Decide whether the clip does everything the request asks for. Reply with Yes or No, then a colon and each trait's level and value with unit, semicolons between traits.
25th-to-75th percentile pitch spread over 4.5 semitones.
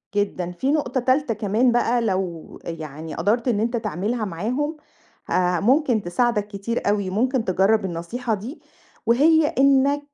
Yes: average, 5.1 semitones